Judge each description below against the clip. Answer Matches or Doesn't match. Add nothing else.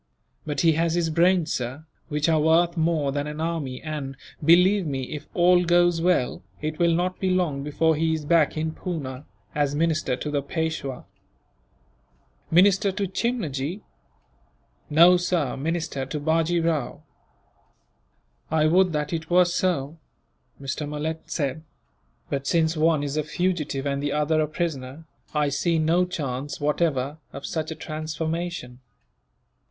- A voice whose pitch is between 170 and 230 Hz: Doesn't match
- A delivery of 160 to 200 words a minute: Doesn't match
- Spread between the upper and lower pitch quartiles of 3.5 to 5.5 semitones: Doesn't match